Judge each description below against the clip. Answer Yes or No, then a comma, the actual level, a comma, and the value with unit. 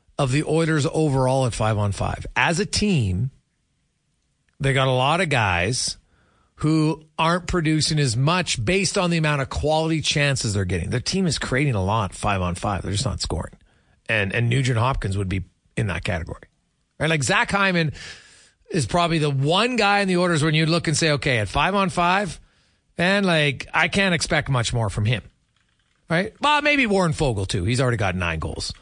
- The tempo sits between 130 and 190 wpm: No, average, 200 wpm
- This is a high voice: No, medium, 140 Hz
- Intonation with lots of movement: Yes, wide, 7.5 semitones